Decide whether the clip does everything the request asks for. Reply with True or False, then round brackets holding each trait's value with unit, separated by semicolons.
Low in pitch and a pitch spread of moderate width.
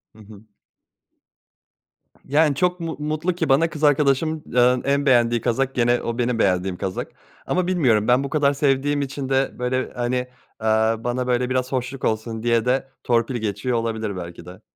True (125 Hz; 3.4 semitones)